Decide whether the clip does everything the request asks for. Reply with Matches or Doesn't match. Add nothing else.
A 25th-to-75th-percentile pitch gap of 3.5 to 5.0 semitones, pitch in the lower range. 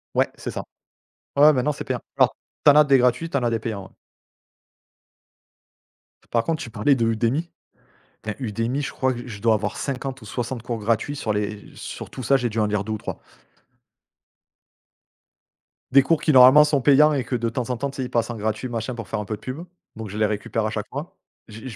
Matches